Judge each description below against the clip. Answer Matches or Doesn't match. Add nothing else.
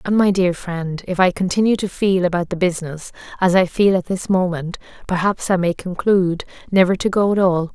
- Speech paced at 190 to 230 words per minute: Matches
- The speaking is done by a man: Doesn't match